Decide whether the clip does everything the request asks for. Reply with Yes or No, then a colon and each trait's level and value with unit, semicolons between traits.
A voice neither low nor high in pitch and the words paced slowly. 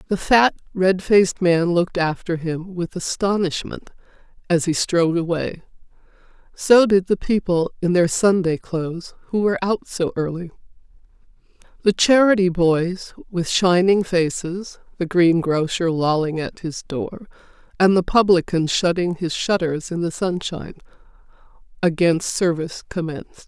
Yes: medium, 175 Hz; slow, 130 wpm